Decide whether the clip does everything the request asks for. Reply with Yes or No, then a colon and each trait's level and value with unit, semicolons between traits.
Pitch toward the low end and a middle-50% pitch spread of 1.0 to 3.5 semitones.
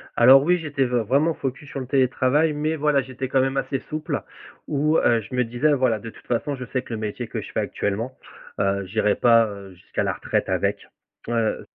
No: low, 130 Hz; average, 4.0 semitones